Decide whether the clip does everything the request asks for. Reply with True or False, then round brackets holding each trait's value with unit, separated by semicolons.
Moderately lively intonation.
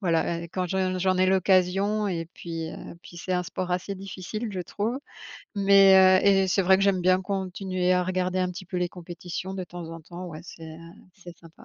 False (1.4 semitones)